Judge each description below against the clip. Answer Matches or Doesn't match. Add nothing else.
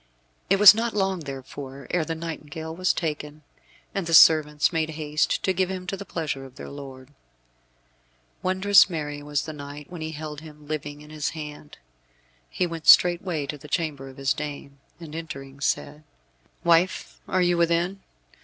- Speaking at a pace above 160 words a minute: Matches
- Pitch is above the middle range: Doesn't match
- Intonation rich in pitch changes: Doesn't match